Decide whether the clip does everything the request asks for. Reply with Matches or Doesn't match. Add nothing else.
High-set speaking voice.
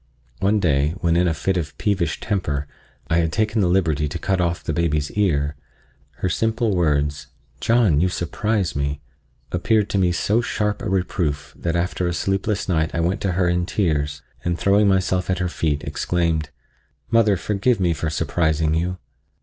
Doesn't match